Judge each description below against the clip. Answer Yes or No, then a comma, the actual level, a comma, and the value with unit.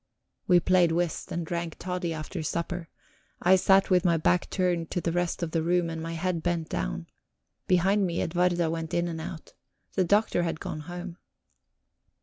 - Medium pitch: Yes, medium, 175 Hz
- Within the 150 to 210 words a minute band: Yes, average, 180 wpm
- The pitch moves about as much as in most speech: No, narrow, 1.6 semitones